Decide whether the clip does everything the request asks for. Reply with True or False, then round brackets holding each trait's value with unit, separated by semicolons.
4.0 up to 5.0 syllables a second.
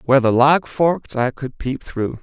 True (4.8 syllables/s)